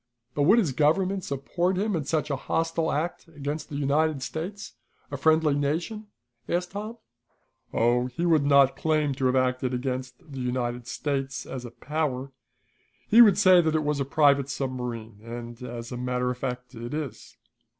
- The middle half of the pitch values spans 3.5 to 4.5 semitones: Yes, average, 4.1 semitones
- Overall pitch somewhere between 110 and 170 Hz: Yes, medium, 140 Hz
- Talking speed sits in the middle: Yes, average, 175 wpm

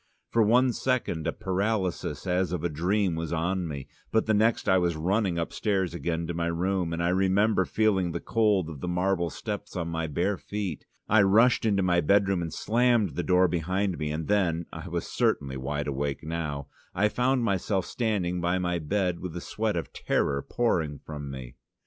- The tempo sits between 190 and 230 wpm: Yes, average, 195 wpm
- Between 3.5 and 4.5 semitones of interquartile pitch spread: Yes, average, 3.8 semitones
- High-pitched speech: No, very low, 90 Hz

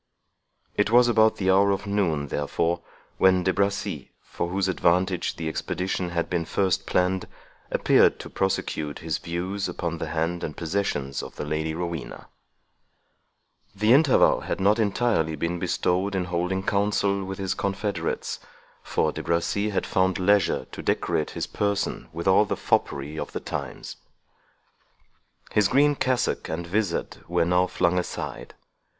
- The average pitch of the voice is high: No, very low, 95 Hz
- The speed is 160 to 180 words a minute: No, average, 150 wpm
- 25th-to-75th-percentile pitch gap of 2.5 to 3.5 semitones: Yes, average, 3.0 semitones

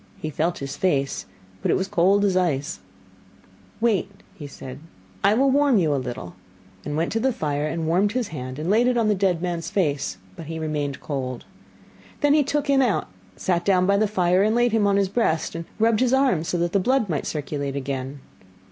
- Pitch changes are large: Yes, wide, 6.5 semitones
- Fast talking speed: Yes, fast, 215 wpm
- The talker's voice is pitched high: No, medium, 180 Hz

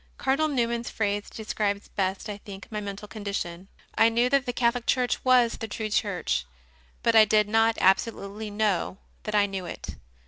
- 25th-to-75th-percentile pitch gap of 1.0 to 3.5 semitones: Yes, narrow, 2.6 semitones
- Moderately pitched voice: No, high, 215 Hz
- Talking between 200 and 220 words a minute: No, average, 180 wpm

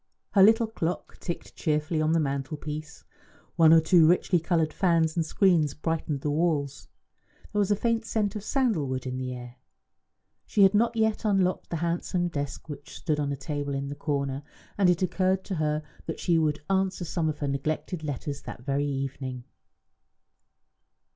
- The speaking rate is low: No, average, 180 wpm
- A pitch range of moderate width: Yes, average, 4.4 semitones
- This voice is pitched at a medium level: Yes, medium, 160 Hz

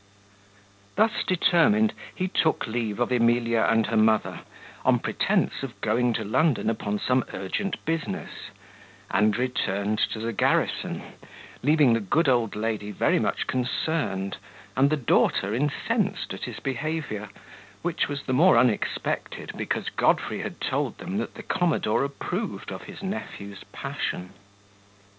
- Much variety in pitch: Yes, wide, 6.5 semitones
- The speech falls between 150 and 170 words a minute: No, average, 140 wpm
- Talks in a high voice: No, low, 125 Hz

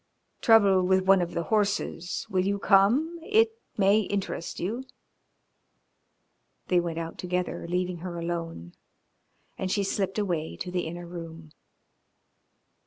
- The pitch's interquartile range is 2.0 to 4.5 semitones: Yes, average, 2.8 semitones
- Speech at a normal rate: No, slow, 130 wpm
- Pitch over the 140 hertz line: Yes, medium, 185 Hz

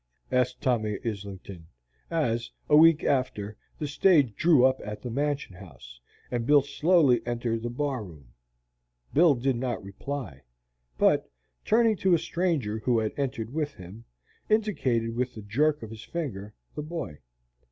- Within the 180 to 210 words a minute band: No, average, 150 wpm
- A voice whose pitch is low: Yes, low, 125 Hz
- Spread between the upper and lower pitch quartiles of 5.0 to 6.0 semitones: Yes, wide, 5.5 semitones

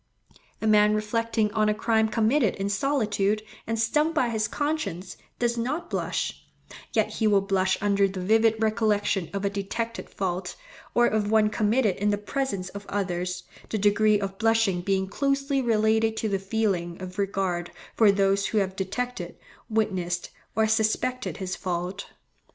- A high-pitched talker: Yes, high, 210 Hz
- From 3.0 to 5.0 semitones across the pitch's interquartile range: No, narrow, 2.5 semitones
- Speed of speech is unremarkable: Yes, average, 160 wpm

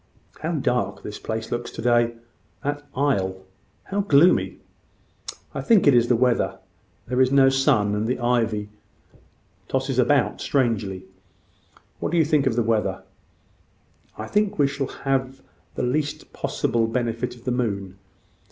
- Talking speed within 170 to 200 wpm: No, average, 150 wpm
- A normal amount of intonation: Yes, average, 3.6 semitones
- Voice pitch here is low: Yes, low, 125 Hz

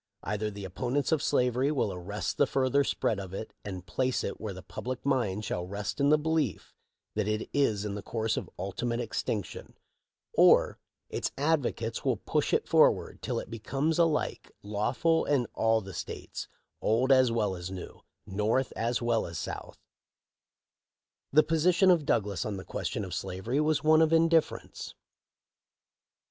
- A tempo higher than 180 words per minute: No, average, 165 wpm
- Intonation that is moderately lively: No, wide, 5.7 semitones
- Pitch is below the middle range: Yes, low, 115 Hz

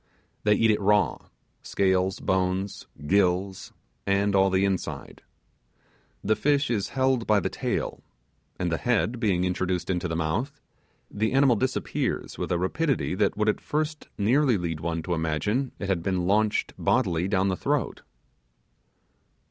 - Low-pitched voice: Yes, low, 100 Hz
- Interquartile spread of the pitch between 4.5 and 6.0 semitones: No, average, 3.6 semitones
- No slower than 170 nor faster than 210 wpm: No, average, 150 wpm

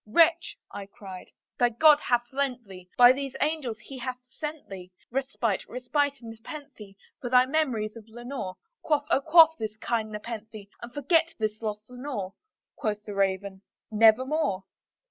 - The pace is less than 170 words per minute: Yes, average, 155 wpm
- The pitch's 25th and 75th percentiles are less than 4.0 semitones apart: No, average, 4.8 semitones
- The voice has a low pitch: No, high, 240 Hz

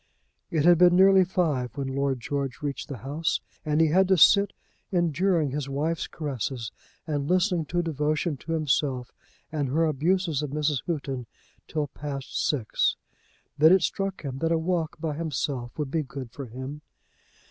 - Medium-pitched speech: Yes, medium, 150 Hz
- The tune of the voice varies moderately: Yes, average, 3.5 semitones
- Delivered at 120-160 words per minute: No, average, 170 wpm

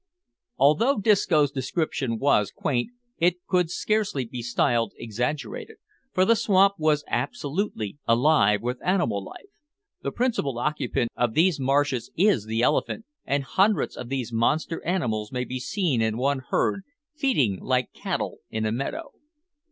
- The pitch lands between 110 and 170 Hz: Yes, medium, 140 Hz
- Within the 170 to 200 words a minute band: No, average, 145 wpm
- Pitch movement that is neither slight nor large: No, wide, 7.1 semitones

